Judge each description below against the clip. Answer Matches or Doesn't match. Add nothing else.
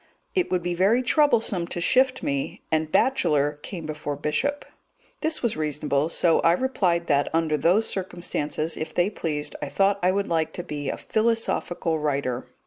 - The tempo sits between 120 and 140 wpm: Doesn't match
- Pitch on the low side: Doesn't match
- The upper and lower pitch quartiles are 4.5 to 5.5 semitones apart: Matches